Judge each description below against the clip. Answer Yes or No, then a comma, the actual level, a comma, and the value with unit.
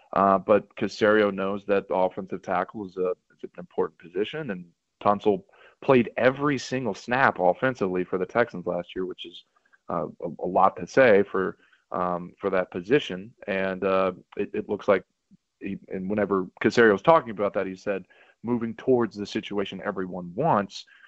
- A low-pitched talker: Yes, very low, 95 Hz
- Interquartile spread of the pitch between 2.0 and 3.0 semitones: Yes, narrow, 2.4 semitones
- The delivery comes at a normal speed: Yes, average, 175 wpm